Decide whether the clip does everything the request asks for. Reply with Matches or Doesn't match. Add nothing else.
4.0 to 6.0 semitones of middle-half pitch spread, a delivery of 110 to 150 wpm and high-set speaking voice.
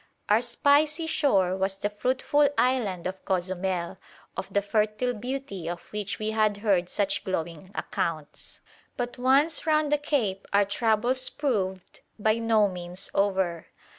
Matches